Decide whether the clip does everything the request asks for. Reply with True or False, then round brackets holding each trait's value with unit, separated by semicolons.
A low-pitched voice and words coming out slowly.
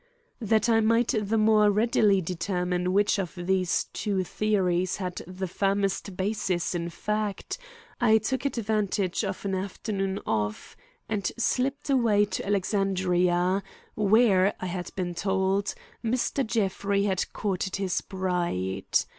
False (195 Hz; 130 wpm)